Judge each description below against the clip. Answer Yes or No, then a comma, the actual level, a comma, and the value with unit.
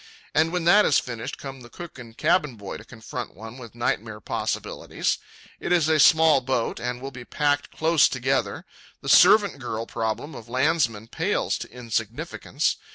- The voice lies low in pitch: Yes, low, 130 Hz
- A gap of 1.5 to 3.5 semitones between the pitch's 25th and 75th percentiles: No, average, 5.1 semitones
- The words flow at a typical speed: Yes, average, 170 wpm